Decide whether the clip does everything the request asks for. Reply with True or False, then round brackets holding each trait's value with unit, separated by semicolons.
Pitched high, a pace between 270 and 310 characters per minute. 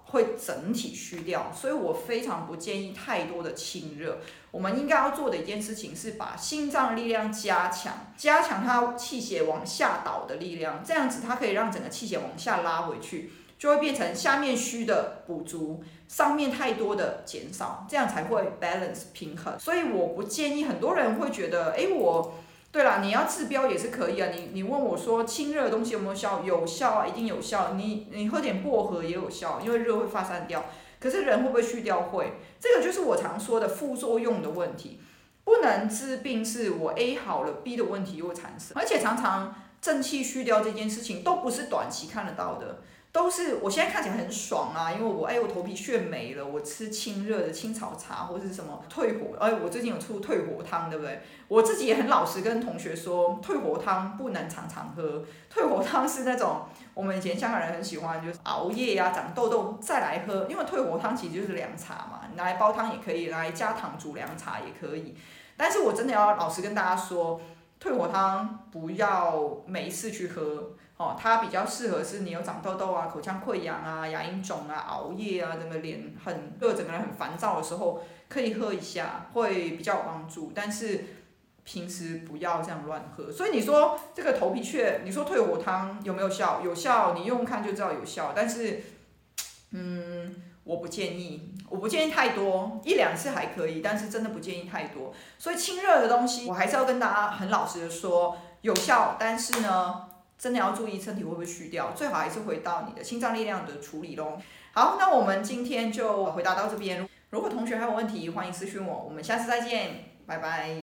True (205 Hz; 305 characters per minute)